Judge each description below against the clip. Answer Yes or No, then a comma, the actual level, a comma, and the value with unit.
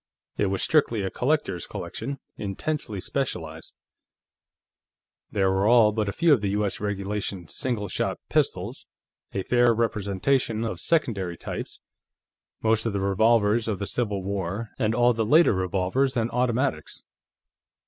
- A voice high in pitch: No, low, 105 Hz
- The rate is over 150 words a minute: No, average, 140 wpm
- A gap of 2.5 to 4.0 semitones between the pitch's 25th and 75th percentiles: Yes, average, 3.7 semitones